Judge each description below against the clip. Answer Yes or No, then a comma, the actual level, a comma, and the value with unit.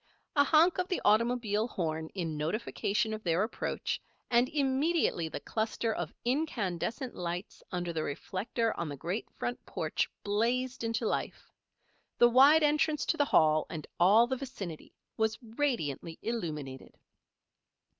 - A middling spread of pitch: No, wide, 6.9 semitones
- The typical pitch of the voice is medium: No, high, 220 Hz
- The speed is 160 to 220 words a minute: No, average, 140 wpm